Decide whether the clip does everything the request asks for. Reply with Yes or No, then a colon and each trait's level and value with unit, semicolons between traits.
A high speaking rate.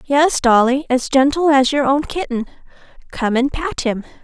No: average, 170 wpm